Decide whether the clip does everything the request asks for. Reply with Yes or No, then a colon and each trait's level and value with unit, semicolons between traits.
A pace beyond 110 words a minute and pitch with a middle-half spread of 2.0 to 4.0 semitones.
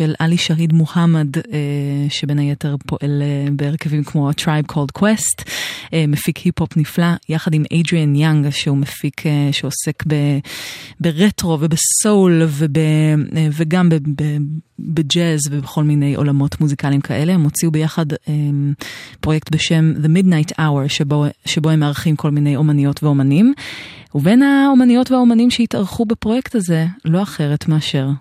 Yes: average, 125 wpm; narrow, 2.4 semitones